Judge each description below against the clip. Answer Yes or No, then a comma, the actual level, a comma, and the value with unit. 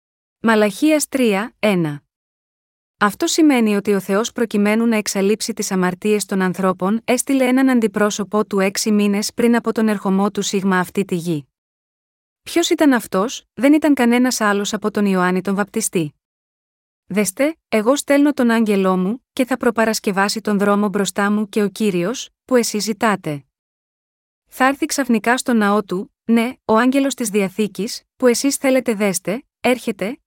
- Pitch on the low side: No, high, 215 Hz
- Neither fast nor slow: Yes, average, 155 wpm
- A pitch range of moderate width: Yes, average, 3.6 semitones